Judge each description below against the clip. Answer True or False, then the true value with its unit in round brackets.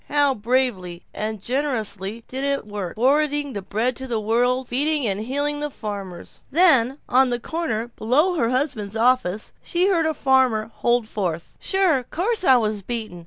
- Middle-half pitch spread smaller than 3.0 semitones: False (5.0 semitones)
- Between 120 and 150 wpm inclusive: False (170 wpm)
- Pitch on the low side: False (250 Hz)